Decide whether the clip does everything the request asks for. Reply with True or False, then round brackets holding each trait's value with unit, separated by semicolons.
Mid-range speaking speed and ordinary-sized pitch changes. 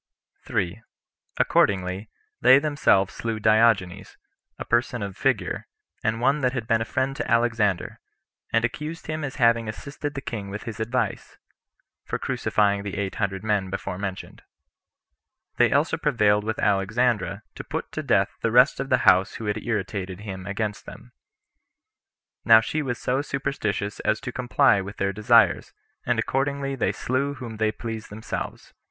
True (155 wpm; 3.9 semitones)